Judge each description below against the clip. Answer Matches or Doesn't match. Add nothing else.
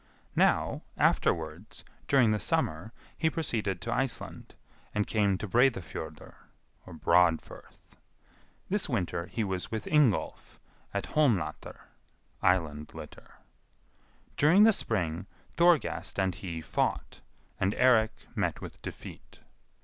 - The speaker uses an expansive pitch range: Matches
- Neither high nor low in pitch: Doesn't match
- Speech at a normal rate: Doesn't match